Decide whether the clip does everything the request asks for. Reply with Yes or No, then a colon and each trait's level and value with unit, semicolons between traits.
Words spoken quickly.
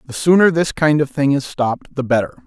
Yes: fast, 245 wpm